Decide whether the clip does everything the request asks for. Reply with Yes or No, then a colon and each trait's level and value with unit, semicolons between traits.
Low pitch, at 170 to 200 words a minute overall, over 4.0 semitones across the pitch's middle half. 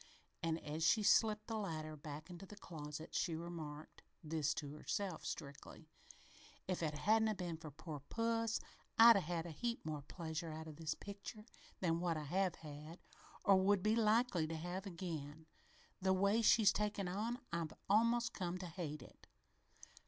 No: medium, 175 Hz; average, 175 wpm; average, 4.7 semitones